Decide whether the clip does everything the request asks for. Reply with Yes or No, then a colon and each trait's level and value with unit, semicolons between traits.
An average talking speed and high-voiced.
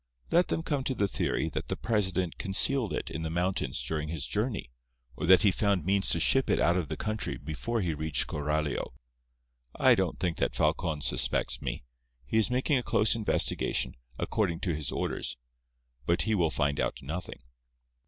No: average, 185 wpm; very low, 90 Hz